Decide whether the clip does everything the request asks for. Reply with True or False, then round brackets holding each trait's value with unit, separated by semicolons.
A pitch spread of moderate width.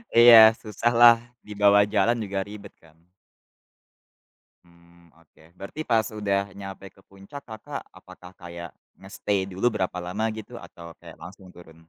True (3.3 semitones)